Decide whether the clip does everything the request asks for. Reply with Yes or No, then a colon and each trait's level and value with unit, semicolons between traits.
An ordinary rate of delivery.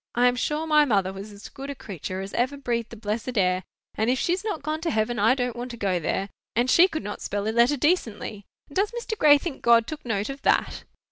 No: fast, 255 wpm